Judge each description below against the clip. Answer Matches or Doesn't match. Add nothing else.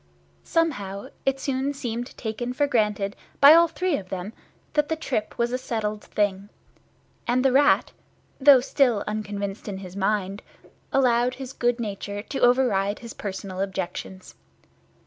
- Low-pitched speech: Doesn't match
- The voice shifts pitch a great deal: Doesn't match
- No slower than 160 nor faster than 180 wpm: Doesn't match